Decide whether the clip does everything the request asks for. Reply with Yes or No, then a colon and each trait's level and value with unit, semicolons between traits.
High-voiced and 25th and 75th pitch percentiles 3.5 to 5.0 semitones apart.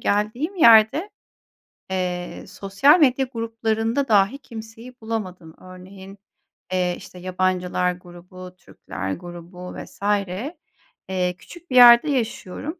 Yes: high, 200 Hz; average, 4.7 semitones